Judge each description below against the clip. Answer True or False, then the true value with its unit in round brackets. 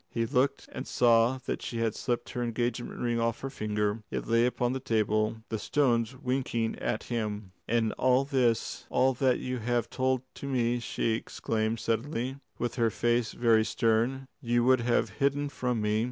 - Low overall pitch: True (120 Hz)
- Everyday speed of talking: True (180 wpm)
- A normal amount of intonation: False (2.1 semitones)